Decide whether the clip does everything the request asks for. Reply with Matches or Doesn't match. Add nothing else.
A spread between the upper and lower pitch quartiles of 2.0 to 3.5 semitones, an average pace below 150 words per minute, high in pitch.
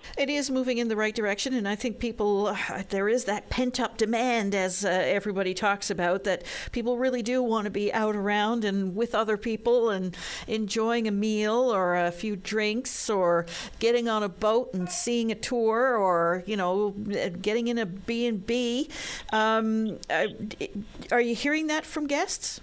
Doesn't match